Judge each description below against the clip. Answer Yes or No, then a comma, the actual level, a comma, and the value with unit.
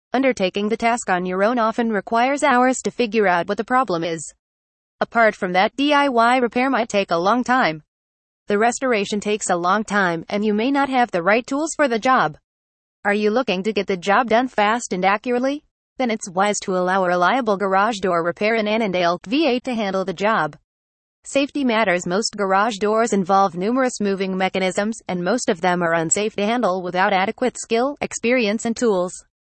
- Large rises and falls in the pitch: No, average, 4.3 semitones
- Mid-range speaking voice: No, high, 205 Hz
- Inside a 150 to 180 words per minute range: No, average, 190 wpm